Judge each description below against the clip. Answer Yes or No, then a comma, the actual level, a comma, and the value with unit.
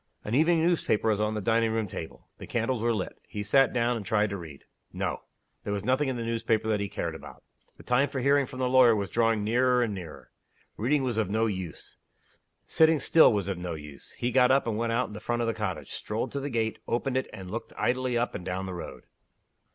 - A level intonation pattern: No, average, 3.7 semitones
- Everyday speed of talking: No, fast, 245 wpm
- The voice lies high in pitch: No, low, 115 Hz